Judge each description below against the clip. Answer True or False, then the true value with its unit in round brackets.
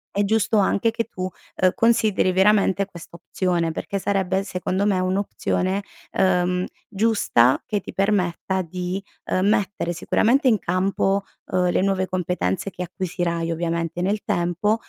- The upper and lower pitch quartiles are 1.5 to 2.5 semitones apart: True (2.1 semitones)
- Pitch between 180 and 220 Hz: True (190 Hz)